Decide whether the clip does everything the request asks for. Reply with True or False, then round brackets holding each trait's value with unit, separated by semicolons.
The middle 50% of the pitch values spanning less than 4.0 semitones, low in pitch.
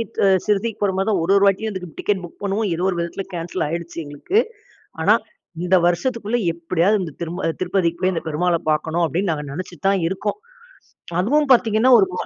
False (3.3 semitones; 185 Hz)